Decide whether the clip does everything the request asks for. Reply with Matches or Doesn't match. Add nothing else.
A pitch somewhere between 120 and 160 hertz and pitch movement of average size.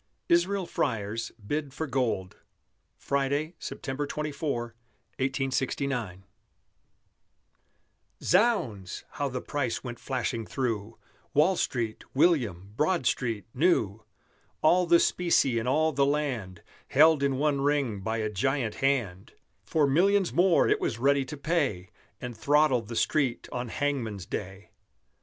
Matches